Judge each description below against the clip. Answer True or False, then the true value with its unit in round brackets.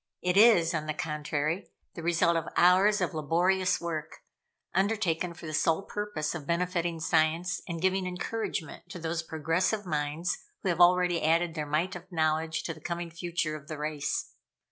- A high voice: False (170 Hz)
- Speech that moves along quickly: False (170 wpm)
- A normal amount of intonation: False (2.3 semitones)